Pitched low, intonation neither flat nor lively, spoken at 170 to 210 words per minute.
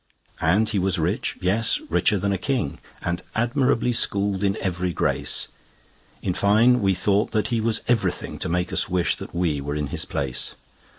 Yes: low, 100 Hz; average, 4.1 semitones; average, 180 wpm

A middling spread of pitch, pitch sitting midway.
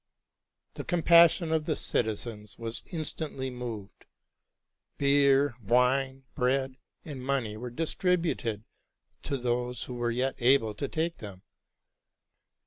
No: average, 3.4 semitones; low, 130 Hz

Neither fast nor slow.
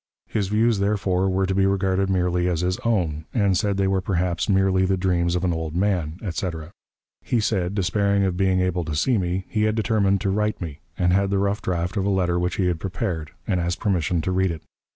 No: fast, 235 wpm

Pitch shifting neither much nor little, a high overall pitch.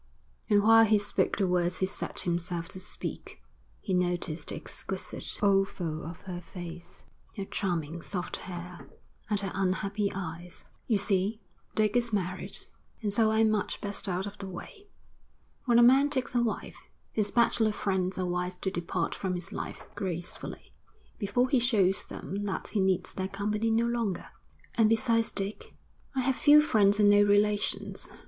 Yes: average, 3.3 semitones; high, 200 Hz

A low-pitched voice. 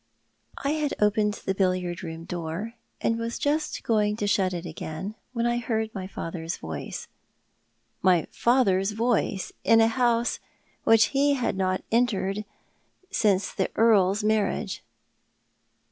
No: high, 210 Hz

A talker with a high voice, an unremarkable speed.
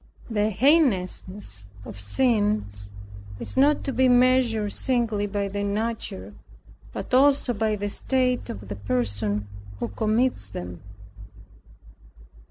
No: high, 210 Hz; slow, 115 wpm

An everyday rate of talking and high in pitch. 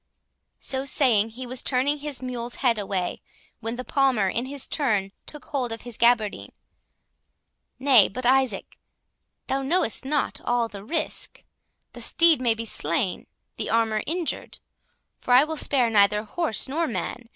Yes: average, 150 wpm; high, 245 Hz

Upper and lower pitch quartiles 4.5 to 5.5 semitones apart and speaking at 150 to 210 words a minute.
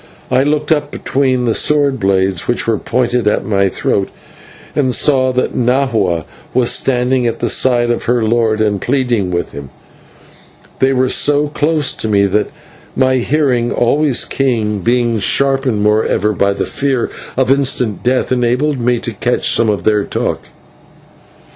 No: average, 3.7 semitones; average, 160 wpm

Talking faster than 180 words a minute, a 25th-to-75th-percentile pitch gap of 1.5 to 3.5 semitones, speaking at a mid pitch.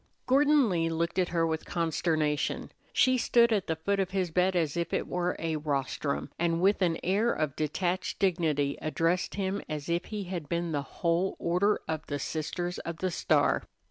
Yes: average, 190 wpm; average, 2.9 semitones; medium, 170 Hz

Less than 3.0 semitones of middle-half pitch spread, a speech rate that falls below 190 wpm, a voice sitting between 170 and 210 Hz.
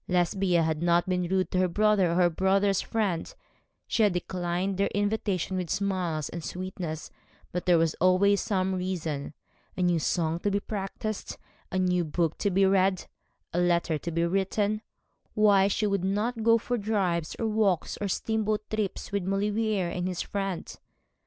Yes: narrow, 2.6 semitones; average, 170 wpm; medium, 185 Hz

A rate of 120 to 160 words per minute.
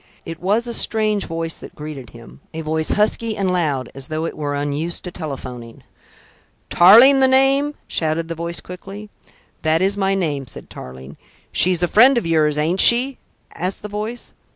No: average, 175 wpm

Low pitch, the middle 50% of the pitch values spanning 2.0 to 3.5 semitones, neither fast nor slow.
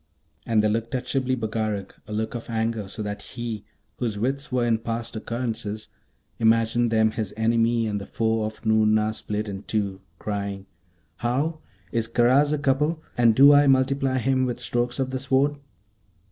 Yes: low, 115 Hz; average, 3.0 semitones; average, 175 wpm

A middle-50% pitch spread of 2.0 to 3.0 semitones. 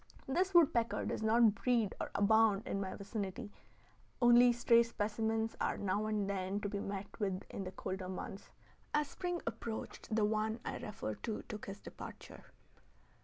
Yes: average, 2.7 semitones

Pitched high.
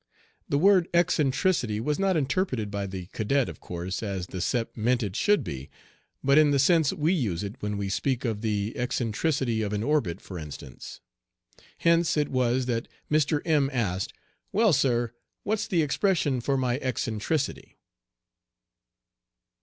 No: low, 125 Hz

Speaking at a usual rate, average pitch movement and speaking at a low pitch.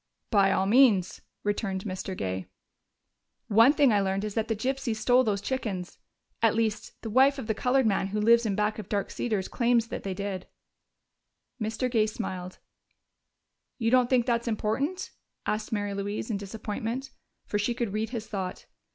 No: average, 175 wpm; average, 3.1 semitones; high, 215 Hz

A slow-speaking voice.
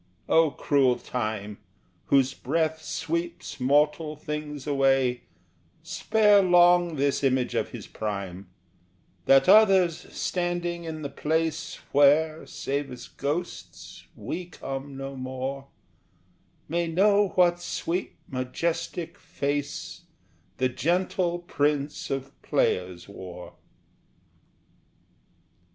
Yes: slow, 100 wpm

